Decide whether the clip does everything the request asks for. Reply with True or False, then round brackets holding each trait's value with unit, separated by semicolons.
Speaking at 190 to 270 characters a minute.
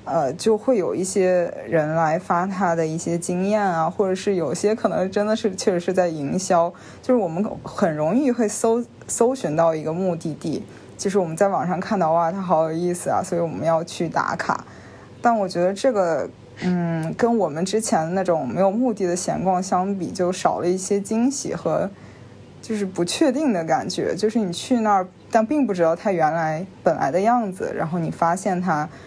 False (285 characters per minute)